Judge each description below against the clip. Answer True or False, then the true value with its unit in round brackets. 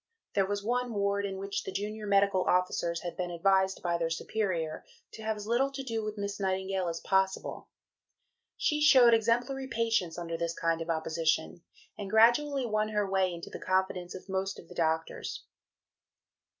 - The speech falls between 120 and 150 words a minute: False (175 wpm)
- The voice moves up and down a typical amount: True (3.8 semitones)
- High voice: True (195 Hz)